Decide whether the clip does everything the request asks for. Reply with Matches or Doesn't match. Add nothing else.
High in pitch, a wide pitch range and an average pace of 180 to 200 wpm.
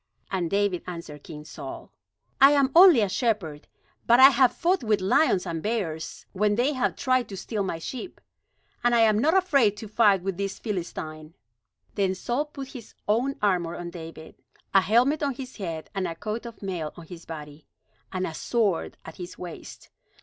Matches